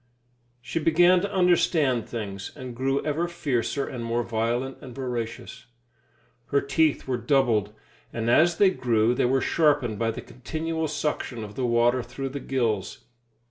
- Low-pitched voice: Yes, low, 130 Hz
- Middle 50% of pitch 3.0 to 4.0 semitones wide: No, average, 4.5 semitones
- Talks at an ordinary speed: Yes, average, 155 wpm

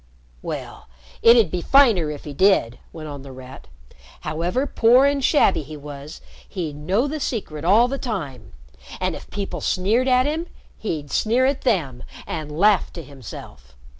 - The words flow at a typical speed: Yes, average, 165 wpm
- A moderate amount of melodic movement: No, wide, 8.6 semitones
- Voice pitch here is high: No, medium, 180 Hz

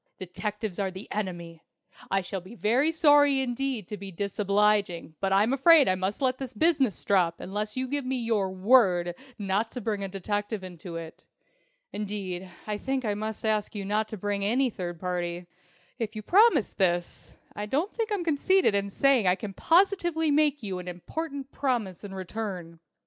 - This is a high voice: Yes, high, 210 Hz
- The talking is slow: No, average, 180 wpm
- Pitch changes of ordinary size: No, wide, 5.8 semitones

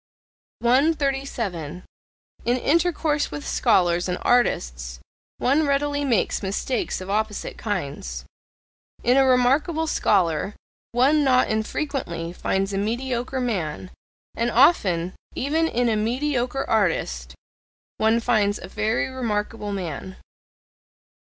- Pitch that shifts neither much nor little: No, wide, 6.2 semitones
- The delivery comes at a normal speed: No, slow, 105 wpm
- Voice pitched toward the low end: No, high, 230 Hz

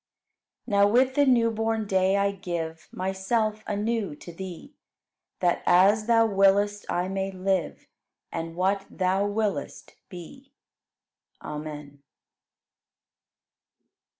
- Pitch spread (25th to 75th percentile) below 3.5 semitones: Yes, average, 3.0 semitones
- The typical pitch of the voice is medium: No, high, 195 Hz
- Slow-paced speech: Yes, slow, 110 wpm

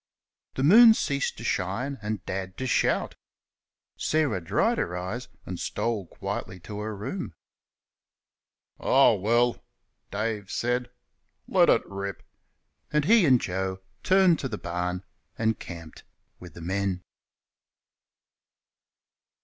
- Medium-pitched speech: No, low, 105 Hz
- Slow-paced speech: Yes, slow, 120 wpm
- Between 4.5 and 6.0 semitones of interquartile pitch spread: Yes, average, 5.3 semitones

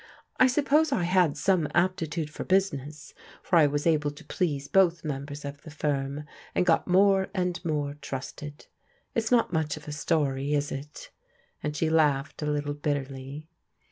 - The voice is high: No, medium, 150 Hz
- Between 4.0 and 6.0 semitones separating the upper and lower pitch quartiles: No, average, 3.5 semitones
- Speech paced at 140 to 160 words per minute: No, average, 170 wpm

